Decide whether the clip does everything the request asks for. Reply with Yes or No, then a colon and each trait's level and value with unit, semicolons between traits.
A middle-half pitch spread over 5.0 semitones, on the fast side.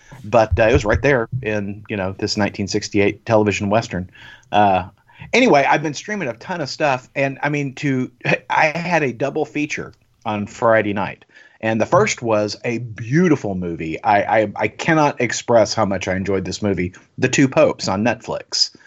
No: wide, 5.4 semitones; average, 180 wpm